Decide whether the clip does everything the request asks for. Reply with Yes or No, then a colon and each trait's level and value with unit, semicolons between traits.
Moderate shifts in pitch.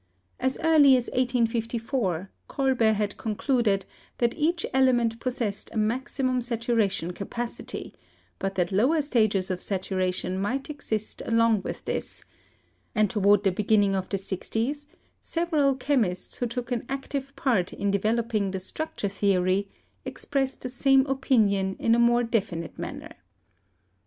Yes: average, 4.7 semitones